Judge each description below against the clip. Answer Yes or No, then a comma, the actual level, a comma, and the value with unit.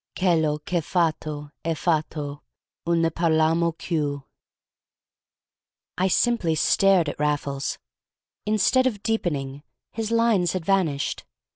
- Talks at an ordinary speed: No, slow, 115 wpm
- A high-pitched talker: No, medium, 165 Hz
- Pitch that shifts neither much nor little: Yes, average, 4.1 semitones